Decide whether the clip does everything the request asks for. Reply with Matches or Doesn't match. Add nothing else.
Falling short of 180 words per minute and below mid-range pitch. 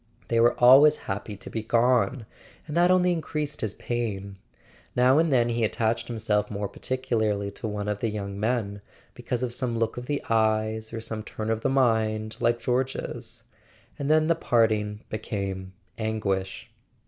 Matches